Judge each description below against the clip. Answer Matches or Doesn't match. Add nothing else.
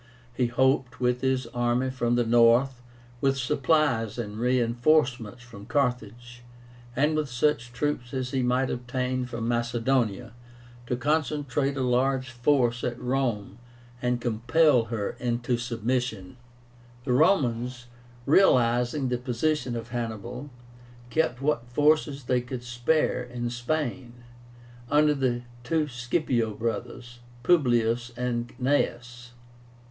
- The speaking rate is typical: Doesn't match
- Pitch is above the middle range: Doesn't match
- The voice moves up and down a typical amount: Doesn't match